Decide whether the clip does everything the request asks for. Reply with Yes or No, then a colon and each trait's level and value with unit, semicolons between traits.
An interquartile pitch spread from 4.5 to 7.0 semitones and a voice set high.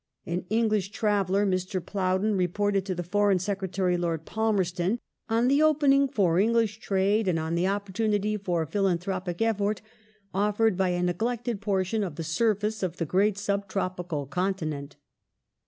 No: average, 2.9 semitones; high, 195 Hz